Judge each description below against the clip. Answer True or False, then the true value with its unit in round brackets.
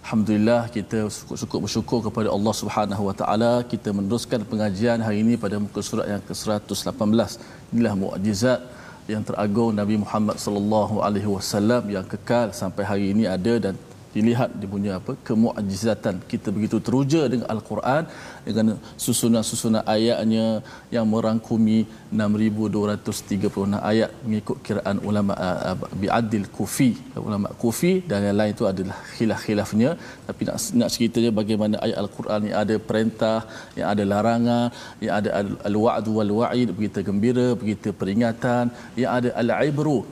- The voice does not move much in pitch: True (2.2 semitones)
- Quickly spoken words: True (140 wpm)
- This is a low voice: True (110 Hz)